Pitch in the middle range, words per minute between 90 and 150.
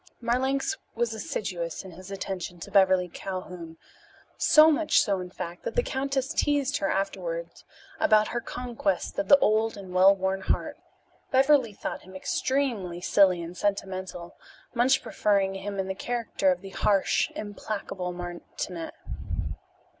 No: high, 195 Hz; average, 145 wpm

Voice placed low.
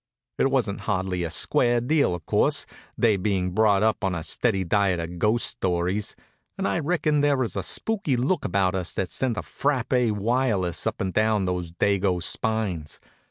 Yes: low, 105 Hz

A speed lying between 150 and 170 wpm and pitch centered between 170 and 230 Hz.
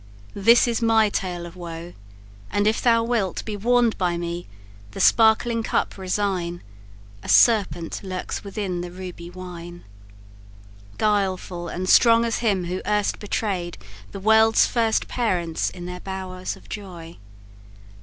No: average, 140 wpm; high, 190 Hz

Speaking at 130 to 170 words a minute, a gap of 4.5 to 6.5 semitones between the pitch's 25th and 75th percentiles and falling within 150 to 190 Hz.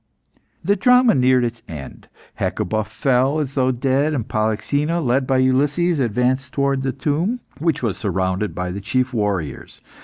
No: average, 155 wpm; average, 4.9 semitones; low, 130 Hz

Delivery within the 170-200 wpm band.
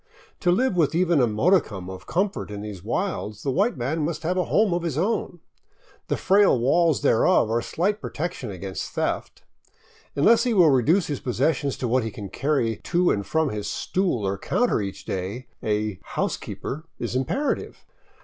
Yes: average, 190 wpm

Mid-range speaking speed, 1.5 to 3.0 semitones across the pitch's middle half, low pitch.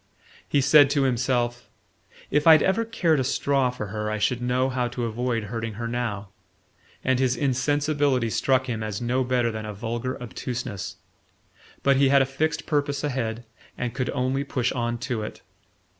Yes: average, 175 wpm; average, 2.7 semitones; low, 125 Hz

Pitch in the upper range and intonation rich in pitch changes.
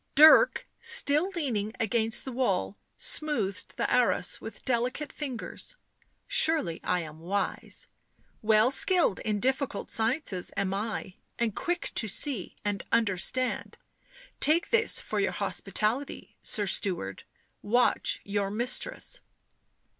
Yes: high, 230 Hz; wide, 6.2 semitones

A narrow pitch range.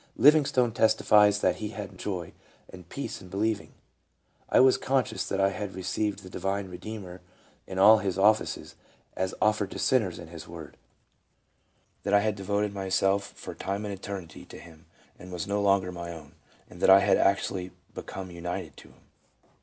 Yes: narrow, 2.3 semitones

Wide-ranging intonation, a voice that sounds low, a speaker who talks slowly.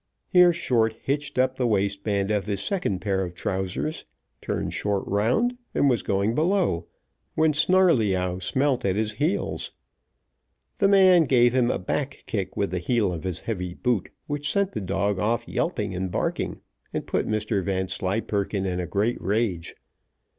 No: wide, 6.3 semitones; low, 105 Hz; average, 160 wpm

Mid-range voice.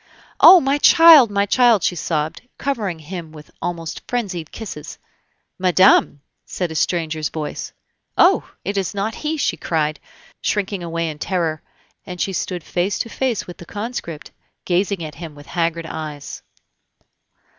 Yes: medium, 175 Hz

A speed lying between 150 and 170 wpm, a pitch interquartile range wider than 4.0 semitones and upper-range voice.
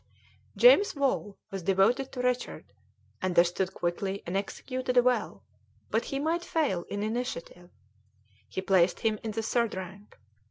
No: slow, 135 wpm; average, 5.1 semitones; high, 215 Hz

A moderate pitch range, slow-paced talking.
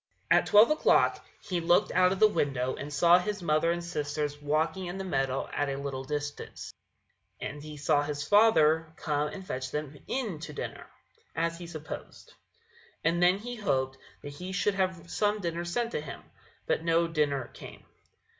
No: average, 3.9 semitones; average, 175 wpm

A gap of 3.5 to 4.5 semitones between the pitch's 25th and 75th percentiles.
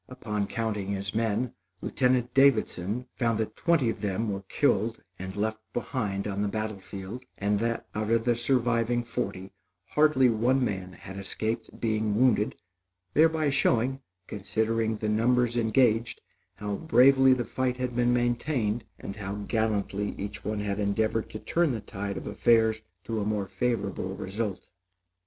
No: average, 3.0 semitones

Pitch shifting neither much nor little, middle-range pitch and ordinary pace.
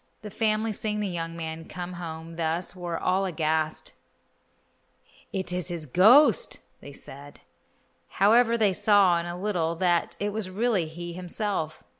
Yes: average, 3.8 semitones; medium, 180 Hz; average, 150 wpm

